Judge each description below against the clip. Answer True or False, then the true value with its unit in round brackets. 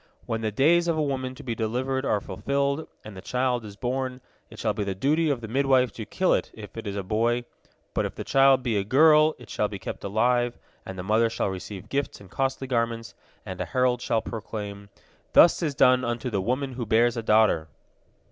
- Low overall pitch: True (120 Hz)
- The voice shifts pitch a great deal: False (3.7 semitones)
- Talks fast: True (225 wpm)